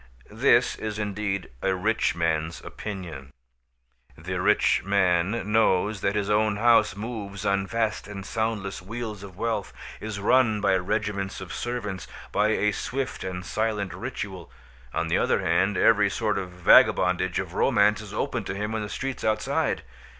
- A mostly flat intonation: Yes, narrow, 2.3 semitones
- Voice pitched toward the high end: No, low, 105 Hz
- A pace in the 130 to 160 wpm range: Yes, average, 155 wpm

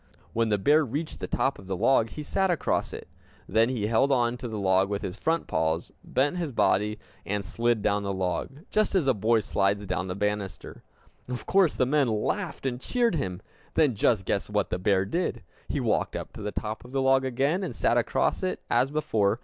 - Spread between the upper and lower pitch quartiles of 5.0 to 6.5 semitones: Yes, wide, 5.6 semitones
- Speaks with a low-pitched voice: Yes, low, 115 Hz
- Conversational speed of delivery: No, fast, 220 wpm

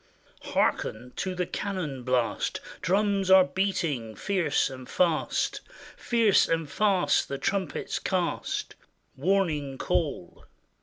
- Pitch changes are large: Yes, wide, 5.8 semitones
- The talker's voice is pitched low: No, medium, 180 Hz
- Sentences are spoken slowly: Yes, slow, 110 wpm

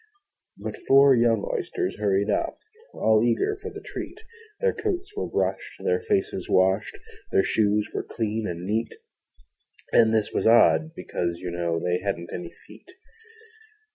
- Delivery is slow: No, average, 150 wpm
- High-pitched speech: No, low, 110 Hz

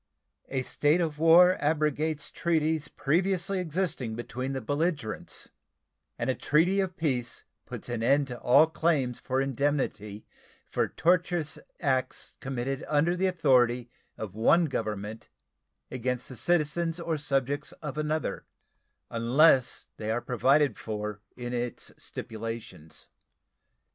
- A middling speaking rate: No, slow, 125 wpm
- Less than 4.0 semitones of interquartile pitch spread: No, average, 4.8 semitones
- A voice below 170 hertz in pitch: Yes, medium, 140 Hz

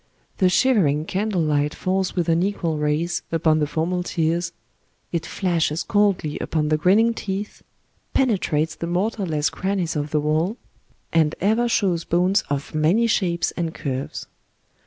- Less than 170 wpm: Yes, average, 140 wpm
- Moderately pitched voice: Yes, medium, 170 Hz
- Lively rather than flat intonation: No, average, 3.8 semitones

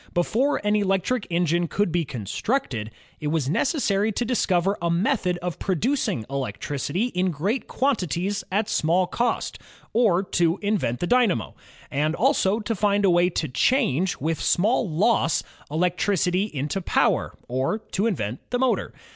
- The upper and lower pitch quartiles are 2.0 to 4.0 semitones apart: No, average, 4.9 semitones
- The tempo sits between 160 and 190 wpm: No, average, 150 wpm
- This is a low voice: No, medium, 185 Hz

